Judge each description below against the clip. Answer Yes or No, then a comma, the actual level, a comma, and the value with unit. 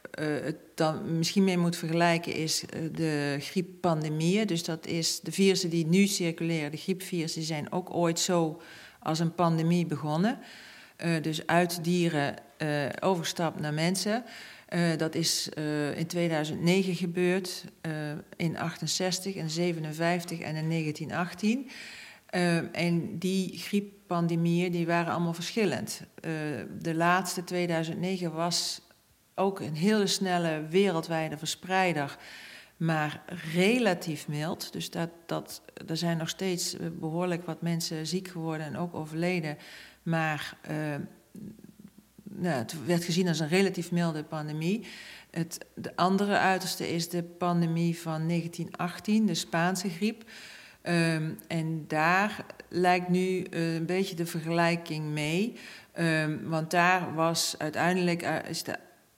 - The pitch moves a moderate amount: No, narrow, 2.2 semitones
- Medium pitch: Yes, medium, 170 Hz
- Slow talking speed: Yes, slow, 130 wpm